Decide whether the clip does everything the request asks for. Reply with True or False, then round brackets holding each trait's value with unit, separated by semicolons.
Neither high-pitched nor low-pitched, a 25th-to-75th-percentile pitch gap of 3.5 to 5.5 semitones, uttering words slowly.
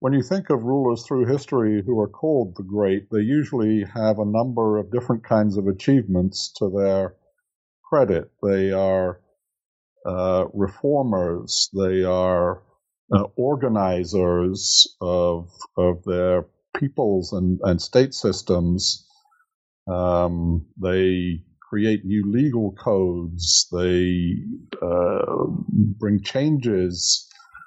False (100 Hz; 4.2 semitones; 110 wpm)